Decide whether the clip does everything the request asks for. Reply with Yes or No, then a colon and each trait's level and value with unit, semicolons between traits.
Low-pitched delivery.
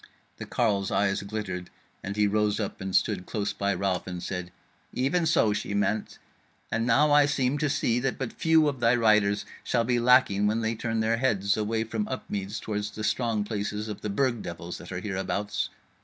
Yes: low, 105 Hz